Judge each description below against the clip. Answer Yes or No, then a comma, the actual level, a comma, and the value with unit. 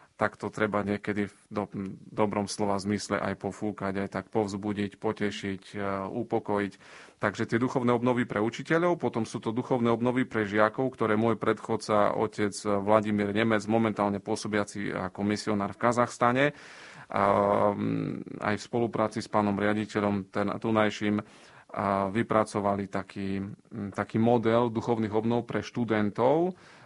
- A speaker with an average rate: Yes, average, 125 wpm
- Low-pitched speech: Yes, low, 105 Hz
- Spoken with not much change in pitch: Yes, narrow, 2.1 semitones